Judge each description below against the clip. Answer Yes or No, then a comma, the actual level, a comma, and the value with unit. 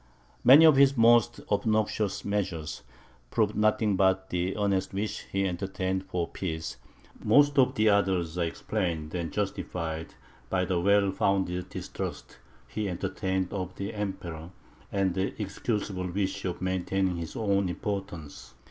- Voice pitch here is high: No, very low, 95 Hz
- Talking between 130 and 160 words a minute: Yes, average, 140 wpm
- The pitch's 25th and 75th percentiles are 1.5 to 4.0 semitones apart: Yes, narrow, 2.6 semitones